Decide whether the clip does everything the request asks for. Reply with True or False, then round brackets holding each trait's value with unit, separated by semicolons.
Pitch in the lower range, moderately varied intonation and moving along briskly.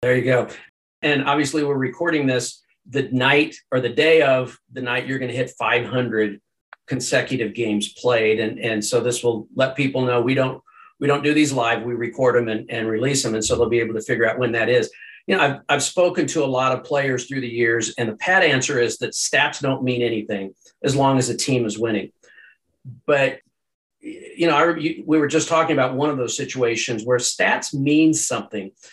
True (130 Hz; 3.3 semitones; 215 wpm)